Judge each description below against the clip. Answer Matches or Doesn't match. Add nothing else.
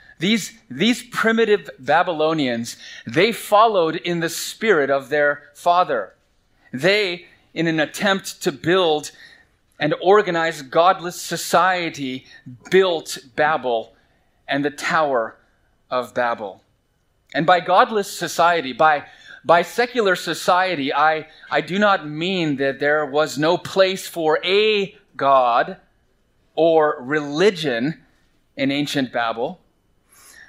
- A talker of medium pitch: Matches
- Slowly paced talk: Matches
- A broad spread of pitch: Doesn't match